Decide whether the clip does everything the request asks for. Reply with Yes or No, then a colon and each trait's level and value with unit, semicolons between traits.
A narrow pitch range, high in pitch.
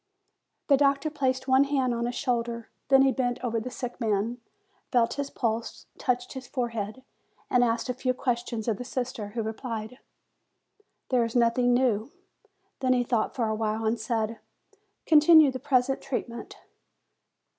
Yes: narrow, 2.3 semitones; high, 245 Hz